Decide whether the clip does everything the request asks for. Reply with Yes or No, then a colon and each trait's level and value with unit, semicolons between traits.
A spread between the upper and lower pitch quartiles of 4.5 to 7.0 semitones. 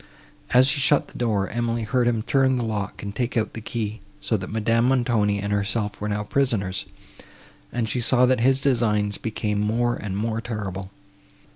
No: average, 2.8 semitones